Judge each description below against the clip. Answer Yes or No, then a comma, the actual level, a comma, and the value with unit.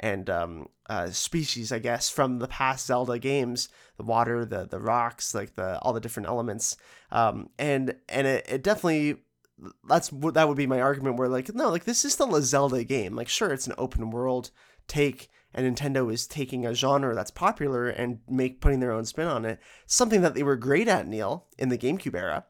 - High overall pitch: No, low, 130 Hz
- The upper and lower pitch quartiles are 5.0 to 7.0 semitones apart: No, average, 3.0 semitones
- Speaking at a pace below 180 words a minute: No, average, 200 wpm